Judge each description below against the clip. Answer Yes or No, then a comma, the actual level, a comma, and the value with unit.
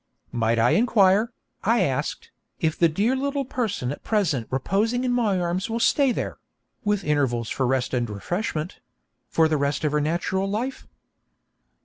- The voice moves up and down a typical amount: No, wide, 8.0 semitones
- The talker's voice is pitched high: No, medium, 180 Hz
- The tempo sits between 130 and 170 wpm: Yes, average, 160 wpm